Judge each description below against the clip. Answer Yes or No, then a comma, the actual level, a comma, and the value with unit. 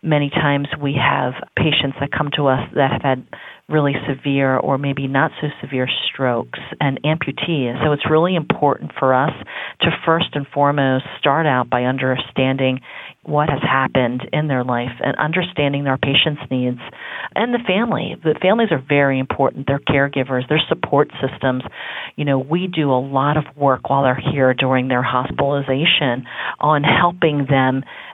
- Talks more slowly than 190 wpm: Yes, average, 165 wpm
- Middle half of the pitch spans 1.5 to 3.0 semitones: Yes, narrow, 2.4 semitones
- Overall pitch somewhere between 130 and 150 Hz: Yes, medium, 140 Hz